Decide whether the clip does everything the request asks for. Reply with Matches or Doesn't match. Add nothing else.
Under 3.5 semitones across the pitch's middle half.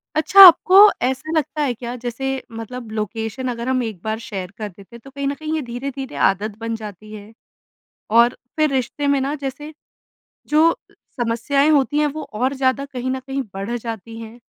Doesn't match